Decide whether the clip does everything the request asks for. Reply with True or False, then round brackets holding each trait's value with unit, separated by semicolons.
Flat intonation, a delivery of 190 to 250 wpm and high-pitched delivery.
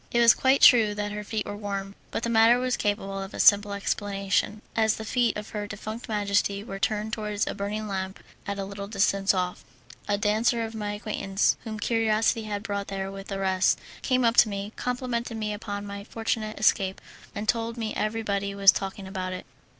True (2.0 semitones; 205 wpm; 210 Hz)